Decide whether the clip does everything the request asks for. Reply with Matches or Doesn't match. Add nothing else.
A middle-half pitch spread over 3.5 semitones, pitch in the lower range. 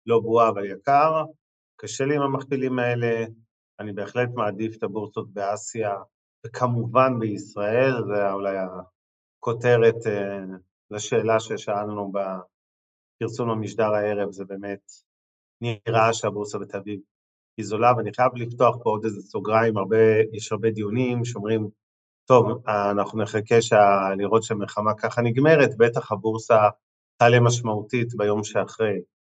Doesn't match